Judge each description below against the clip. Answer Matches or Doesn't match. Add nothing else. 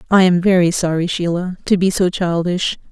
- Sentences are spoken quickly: Doesn't match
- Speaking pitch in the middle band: Matches